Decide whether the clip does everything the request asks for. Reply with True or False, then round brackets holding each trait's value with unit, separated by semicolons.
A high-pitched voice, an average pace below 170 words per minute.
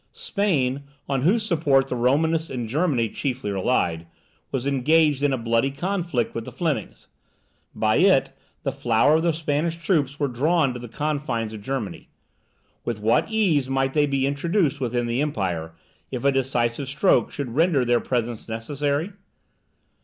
False (135 Hz; 160 wpm)